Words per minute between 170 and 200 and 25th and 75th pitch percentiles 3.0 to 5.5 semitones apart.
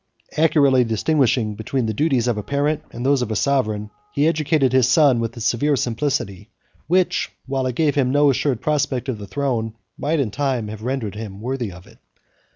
Yes: average, 195 wpm; average, 4.2 semitones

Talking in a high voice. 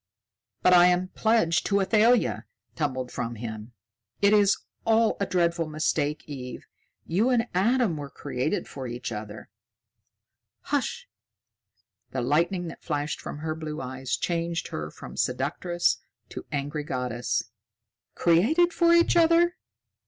No: medium, 165 Hz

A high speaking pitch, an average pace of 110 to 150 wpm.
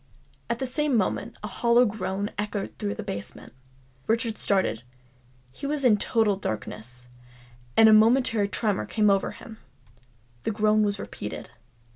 Yes: high, 210 Hz; average, 140 wpm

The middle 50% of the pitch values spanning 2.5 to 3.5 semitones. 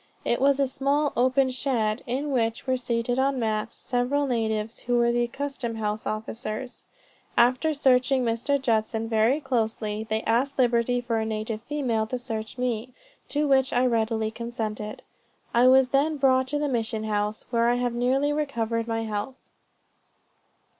Yes: average, 2.9 semitones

